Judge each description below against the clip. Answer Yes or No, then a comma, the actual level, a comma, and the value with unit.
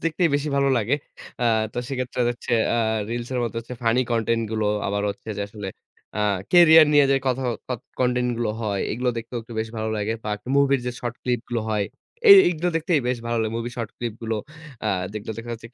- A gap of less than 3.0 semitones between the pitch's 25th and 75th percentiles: Yes, narrow, 2.6 semitones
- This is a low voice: Yes, low, 120 Hz